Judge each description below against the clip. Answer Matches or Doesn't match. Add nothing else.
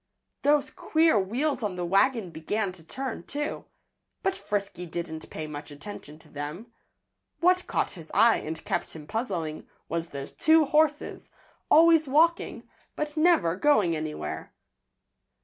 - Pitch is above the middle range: Matches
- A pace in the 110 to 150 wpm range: Matches